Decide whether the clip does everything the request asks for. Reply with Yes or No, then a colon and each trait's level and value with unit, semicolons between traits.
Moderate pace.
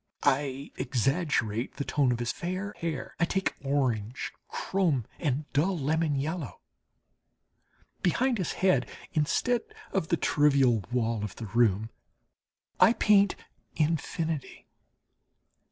No: slow, 115 wpm